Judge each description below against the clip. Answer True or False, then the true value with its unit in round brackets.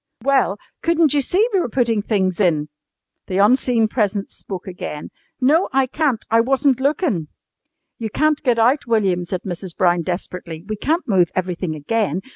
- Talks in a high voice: True (220 Hz)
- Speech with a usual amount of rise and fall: False (6.7 semitones)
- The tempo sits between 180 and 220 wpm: False (165 wpm)